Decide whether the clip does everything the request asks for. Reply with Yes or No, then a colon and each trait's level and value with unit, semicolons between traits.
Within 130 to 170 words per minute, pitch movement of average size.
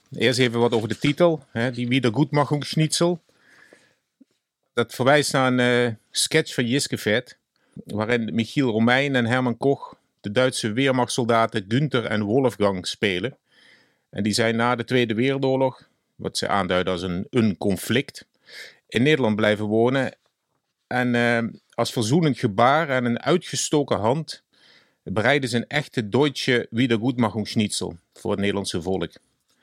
Yes: slow, 135 wpm; average, 3.7 semitones